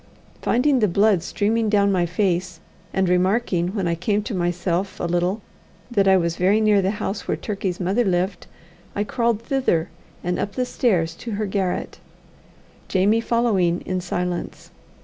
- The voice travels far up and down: No, average, 3.2 semitones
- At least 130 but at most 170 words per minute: Yes, average, 165 wpm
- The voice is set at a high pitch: Yes, high, 195 Hz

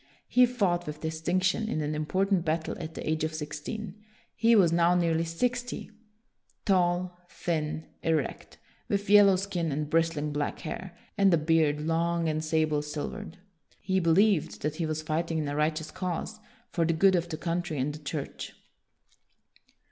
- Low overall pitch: No, medium, 165 Hz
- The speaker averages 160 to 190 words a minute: Yes, average, 165 wpm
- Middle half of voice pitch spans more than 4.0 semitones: No, average, 3.0 semitones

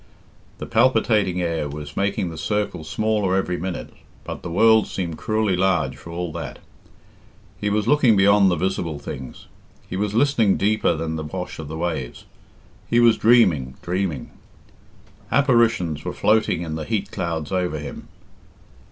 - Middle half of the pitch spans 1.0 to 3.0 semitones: No, average, 4.9 semitones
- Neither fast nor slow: Yes, average, 155 wpm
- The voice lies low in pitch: Yes, very low, 90 Hz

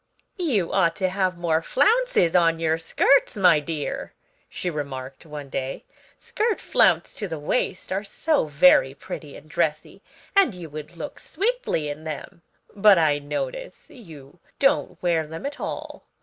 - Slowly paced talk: No, average, 155 wpm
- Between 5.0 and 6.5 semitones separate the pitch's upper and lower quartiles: Yes, wide, 5.4 semitones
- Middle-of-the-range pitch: Yes, medium, 170 Hz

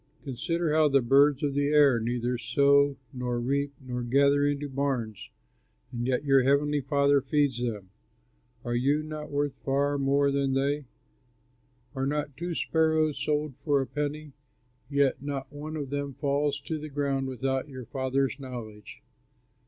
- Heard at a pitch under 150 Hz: Yes, medium, 140 Hz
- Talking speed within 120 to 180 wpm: Yes, average, 155 wpm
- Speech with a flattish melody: Yes, narrow, 1.8 semitones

